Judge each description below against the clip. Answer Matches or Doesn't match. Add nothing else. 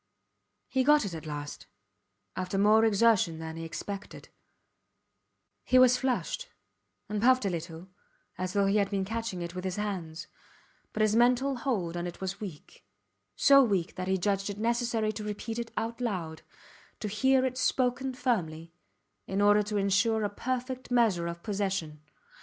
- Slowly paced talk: Doesn't match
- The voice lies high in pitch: Matches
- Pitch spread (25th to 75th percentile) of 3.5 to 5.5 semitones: Matches